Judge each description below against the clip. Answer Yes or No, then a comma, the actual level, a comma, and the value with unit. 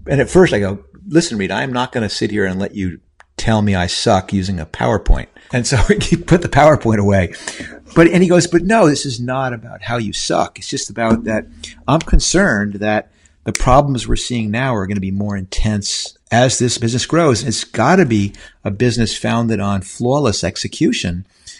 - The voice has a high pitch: No, low, 110 Hz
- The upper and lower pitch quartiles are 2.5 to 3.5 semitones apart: No, average, 4.3 semitones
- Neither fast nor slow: No, fast, 210 wpm